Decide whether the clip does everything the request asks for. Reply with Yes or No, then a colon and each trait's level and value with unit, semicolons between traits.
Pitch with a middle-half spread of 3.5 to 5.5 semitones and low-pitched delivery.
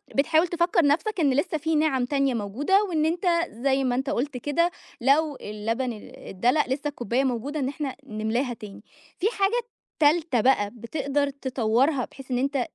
No: average, 4.0 semitones; very high, 275 Hz